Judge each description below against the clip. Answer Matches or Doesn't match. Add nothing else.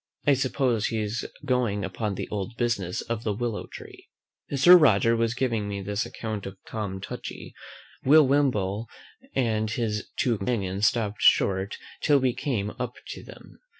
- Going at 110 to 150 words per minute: Doesn't match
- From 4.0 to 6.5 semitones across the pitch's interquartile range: Doesn't match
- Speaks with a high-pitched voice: Doesn't match